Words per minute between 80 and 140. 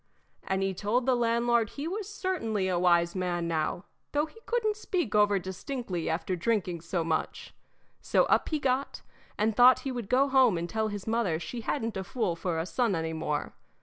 No: average, 195 wpm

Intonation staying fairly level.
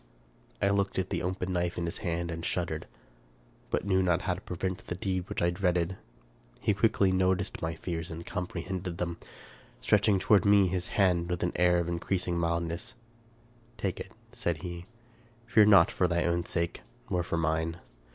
Yes: narrow, 2.1 semitones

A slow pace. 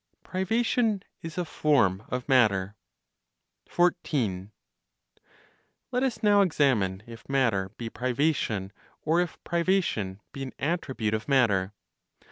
Yes: slow, 110 wpm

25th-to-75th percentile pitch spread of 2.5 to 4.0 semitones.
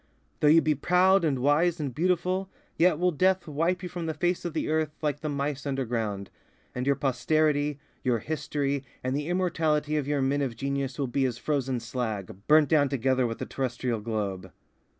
Yes: average, 3.6 semitones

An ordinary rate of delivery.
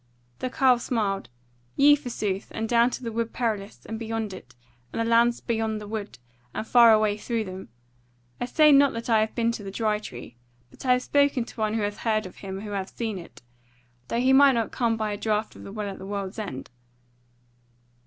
No: fast, 220 wpm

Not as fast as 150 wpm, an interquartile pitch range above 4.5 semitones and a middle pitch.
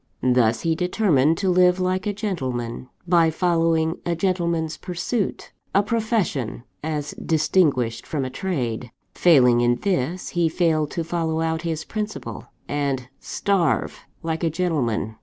Yes: average, 140 wpm; average, 5.1 semitones; medium, 160 Hz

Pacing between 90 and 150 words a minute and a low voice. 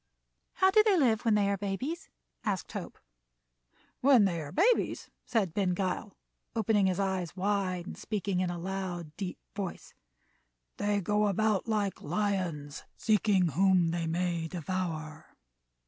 No: average, 145 wpm; high, 195 Hz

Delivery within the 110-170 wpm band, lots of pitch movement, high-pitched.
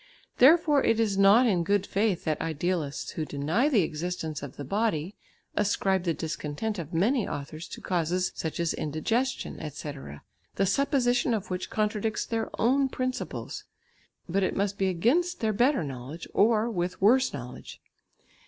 Yes: average, 155 wpm; wide, 6.1 semitones; high, 195 Hz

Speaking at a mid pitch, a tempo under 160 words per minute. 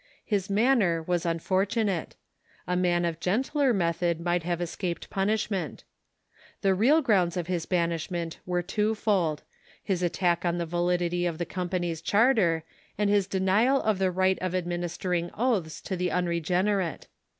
Yes: medium, 180 Hz; average, 145 wpm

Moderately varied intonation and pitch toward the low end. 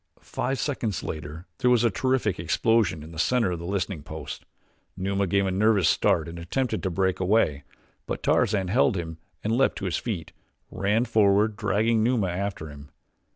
Yes: average, 4.7 semitones; low, 100 Hz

